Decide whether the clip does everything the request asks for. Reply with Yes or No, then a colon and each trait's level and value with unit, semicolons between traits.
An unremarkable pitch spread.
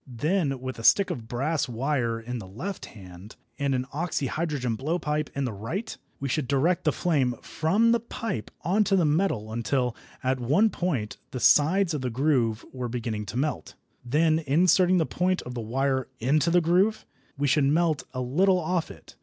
No: wide, 5.7 semitones